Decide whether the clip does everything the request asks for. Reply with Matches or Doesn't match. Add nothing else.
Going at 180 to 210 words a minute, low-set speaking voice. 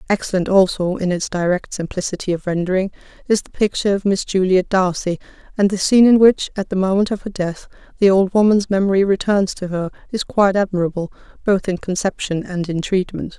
Doesn't match